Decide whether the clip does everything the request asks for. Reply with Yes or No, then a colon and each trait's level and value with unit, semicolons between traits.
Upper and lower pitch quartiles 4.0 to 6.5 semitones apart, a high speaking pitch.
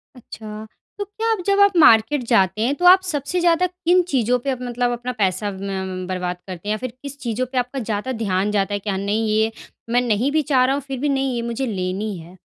Yes: wide, 5.4 semitones; high, 240 Hz